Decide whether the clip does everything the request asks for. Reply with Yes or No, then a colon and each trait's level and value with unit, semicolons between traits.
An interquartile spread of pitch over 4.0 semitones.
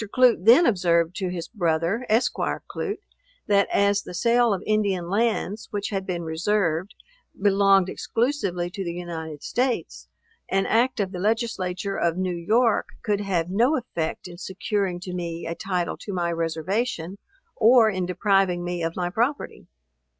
No: average, 3.7 semitones